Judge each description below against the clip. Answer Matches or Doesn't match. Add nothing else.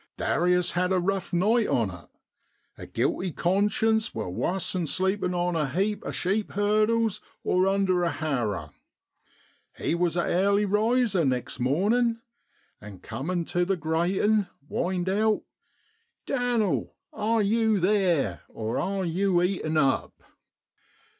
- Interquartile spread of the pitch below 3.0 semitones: Doesn't match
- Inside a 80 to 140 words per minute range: Matches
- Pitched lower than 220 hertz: Matches